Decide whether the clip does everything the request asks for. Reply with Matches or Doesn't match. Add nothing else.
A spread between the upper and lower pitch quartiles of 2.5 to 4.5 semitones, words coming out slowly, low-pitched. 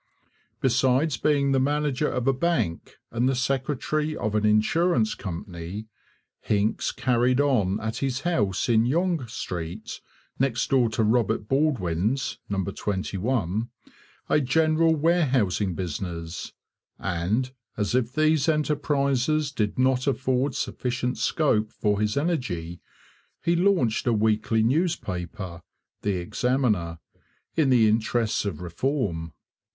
Doesn't match